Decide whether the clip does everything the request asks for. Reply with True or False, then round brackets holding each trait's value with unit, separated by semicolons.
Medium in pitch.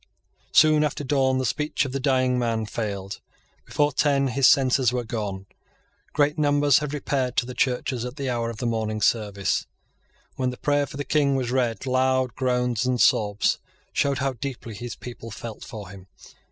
False (125 Hz)